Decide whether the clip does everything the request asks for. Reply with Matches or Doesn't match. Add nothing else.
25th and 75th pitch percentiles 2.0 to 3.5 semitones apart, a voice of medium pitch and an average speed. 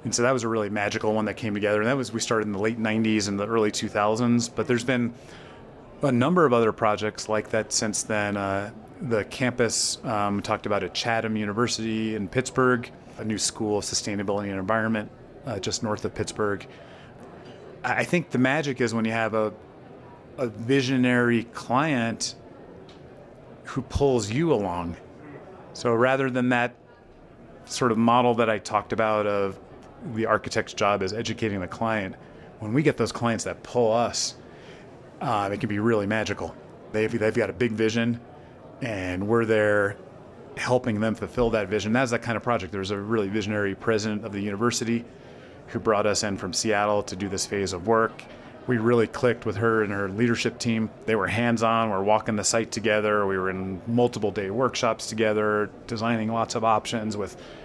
Doesn't match